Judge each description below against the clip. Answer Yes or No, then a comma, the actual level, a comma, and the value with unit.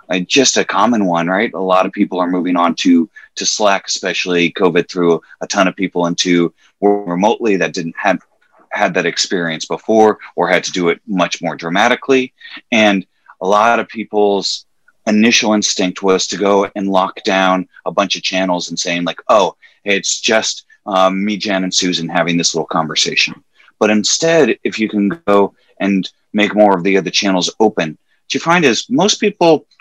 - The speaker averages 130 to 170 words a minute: No, average, 185 wpm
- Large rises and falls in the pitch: No, average, 2.8 semitones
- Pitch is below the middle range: Yes, very low, 95 Hz